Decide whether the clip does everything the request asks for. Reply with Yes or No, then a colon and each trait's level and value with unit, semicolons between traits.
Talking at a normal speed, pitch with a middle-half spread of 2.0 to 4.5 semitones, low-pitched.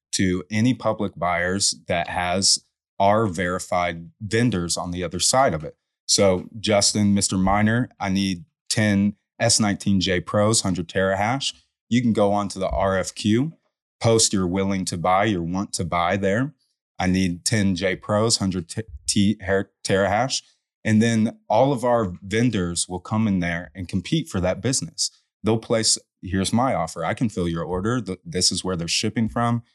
Yes: average, 165 wpm; average, 3.3 semitones; low, 100 Hz